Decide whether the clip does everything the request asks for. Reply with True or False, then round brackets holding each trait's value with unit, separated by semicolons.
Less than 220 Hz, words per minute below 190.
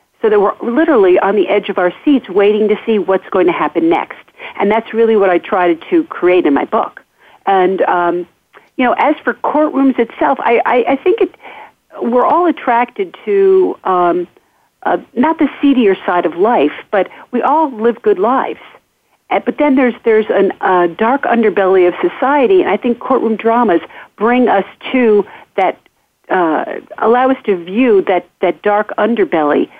False (230 Hz; 180 wpm)